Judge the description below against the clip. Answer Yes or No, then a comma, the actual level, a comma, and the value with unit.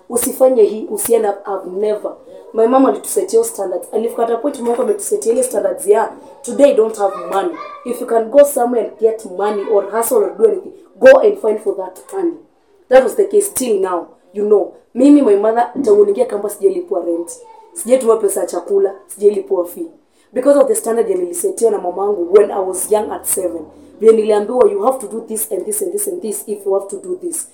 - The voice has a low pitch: No, very high, 260 Hz